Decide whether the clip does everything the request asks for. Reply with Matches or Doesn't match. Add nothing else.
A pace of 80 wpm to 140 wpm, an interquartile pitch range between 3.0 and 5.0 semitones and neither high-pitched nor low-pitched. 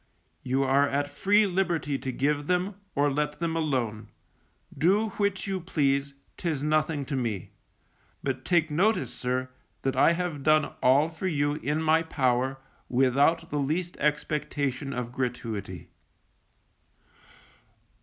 Matches